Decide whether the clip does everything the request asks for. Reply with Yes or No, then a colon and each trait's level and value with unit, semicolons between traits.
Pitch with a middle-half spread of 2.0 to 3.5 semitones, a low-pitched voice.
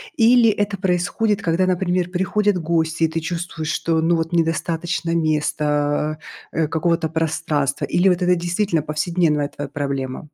No: narrow, 2.6 semitones; medium, 165 Hz